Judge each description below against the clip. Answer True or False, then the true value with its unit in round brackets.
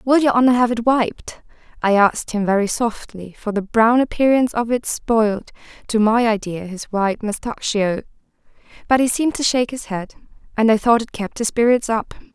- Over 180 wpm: True (190 wpm)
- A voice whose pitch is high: True (225 Hz)